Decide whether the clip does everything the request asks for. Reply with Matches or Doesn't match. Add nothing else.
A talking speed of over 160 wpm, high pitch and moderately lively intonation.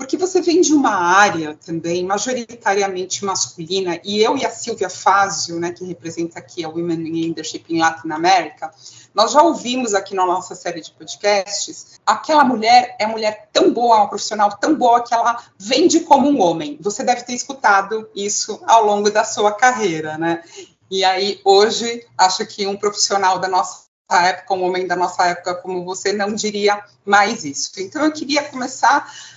Matches